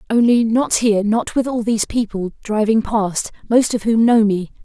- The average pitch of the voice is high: Yes, high, 220 Hz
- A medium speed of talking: Yes, average, 195 wpm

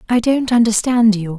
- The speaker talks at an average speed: Yes, average, 175 wpm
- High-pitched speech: Yes, high, 225 Hz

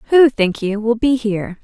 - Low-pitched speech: No, high, 230 Hz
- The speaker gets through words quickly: Yes, fast, 220 wpm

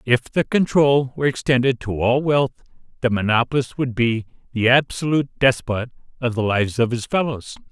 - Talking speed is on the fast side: No, average, 165 wpm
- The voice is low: Yes, low, 125 Hz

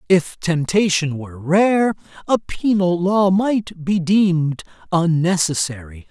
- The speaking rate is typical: No, slow, 110 wpm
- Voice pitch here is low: No, medium, 175 Hz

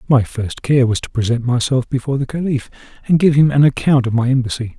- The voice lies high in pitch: No, low, 130 Hz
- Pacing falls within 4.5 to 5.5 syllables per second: No, 6.1 syllables/s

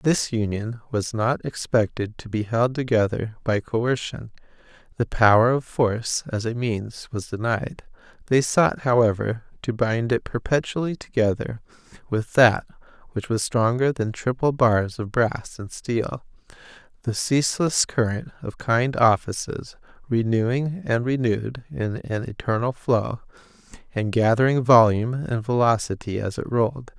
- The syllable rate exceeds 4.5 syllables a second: No, 4.4 syllables/s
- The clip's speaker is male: Yes, male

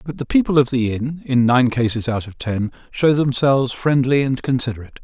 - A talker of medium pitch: No, low, 130 Hz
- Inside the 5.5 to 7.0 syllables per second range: Yes, 5.6 syllables/s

